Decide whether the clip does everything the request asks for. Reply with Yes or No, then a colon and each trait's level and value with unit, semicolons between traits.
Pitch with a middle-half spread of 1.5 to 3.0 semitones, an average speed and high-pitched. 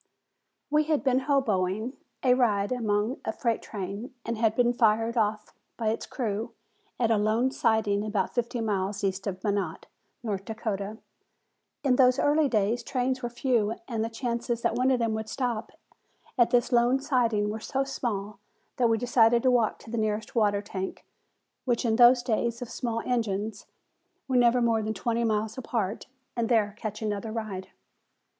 Yes: average, 2.7 semitones; average, 175 wpm; high, 225 Hz